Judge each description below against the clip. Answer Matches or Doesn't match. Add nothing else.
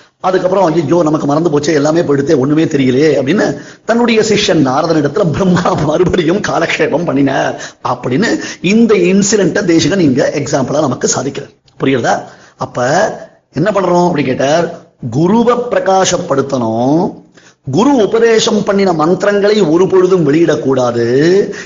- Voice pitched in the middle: Matches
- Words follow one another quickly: Doesn't match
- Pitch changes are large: Doesn't match